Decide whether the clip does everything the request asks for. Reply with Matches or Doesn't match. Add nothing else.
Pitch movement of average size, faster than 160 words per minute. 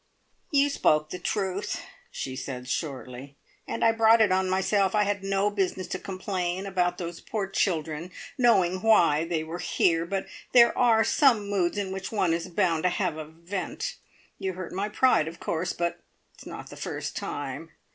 Matches